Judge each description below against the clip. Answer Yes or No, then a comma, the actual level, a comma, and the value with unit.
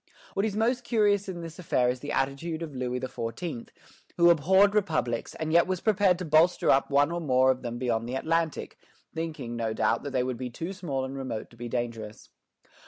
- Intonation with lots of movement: Yes, wide, 5.7 semitones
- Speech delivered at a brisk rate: Yes, fast, 210 wpm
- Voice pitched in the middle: Yes, medium, 145 Hz